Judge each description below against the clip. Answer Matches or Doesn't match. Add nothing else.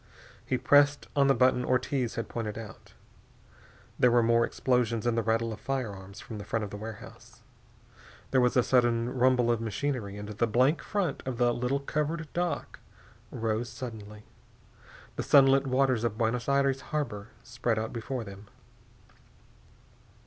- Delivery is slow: Doesn't match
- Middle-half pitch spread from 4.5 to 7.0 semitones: Doesn't match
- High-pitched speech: Doesn't match